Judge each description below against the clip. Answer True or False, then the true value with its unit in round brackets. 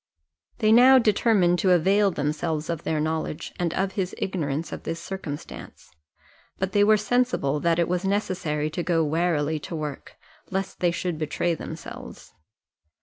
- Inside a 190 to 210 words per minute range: False (155 wpm)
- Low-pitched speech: False (175 Hz)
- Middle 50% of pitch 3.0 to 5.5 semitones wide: True (3.8 semitones)